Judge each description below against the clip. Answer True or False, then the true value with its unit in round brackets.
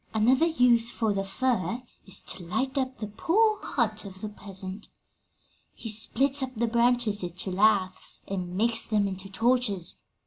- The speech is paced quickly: False (160 wpm)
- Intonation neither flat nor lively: True (4.2 semitones)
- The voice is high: True (220 Hz)